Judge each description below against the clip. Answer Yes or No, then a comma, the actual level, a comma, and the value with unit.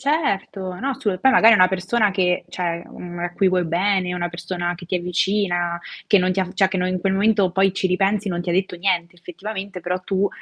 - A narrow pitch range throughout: Yes, narrow, 2.0 semitones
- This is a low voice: No, medium, 185 Hz